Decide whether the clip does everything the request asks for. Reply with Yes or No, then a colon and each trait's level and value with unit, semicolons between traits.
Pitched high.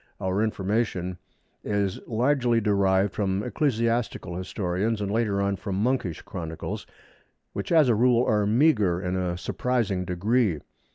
No: low, 105 Hz